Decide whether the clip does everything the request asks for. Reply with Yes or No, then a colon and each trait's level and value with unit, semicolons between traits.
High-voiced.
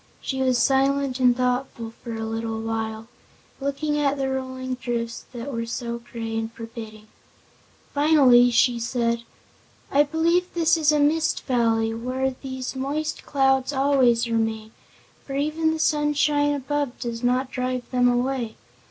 Yes: very high, 255 Hz